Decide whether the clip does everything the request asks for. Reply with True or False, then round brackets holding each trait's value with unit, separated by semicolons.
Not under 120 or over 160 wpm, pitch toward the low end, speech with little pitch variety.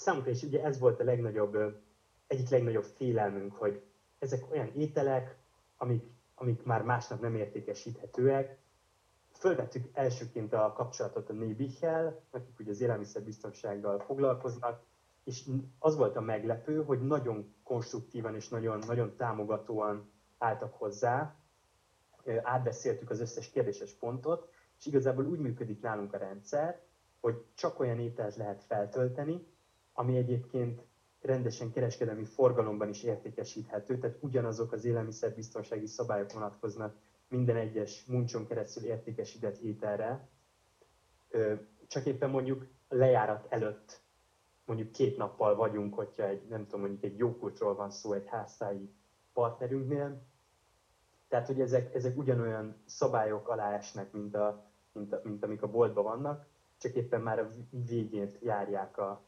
False (130 wpm; 115 Hz; 3.7 semitones)